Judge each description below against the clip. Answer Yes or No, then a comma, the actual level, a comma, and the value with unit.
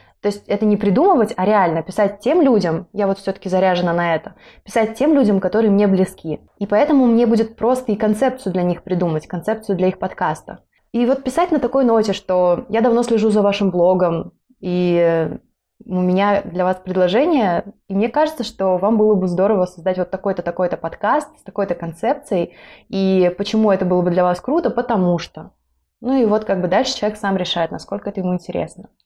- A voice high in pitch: Yes, high, 200 Hz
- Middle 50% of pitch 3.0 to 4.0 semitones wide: Yes, average, 3.6 semitones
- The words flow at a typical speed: No, fast, 195 wpm